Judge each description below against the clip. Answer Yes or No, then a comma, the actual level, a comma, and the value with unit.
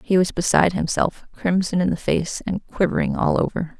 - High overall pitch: No, medium, 180 Hz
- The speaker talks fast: No, average, 190 wpm